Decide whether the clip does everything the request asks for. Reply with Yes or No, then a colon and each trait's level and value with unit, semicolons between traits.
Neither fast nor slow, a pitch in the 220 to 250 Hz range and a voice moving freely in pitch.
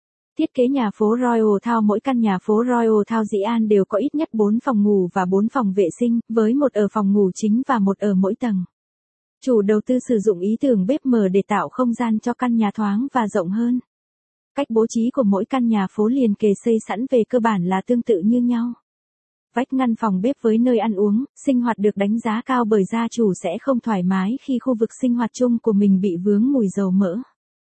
No: average, 240 wpm; high, 225 Hz; average, 3.0 semitones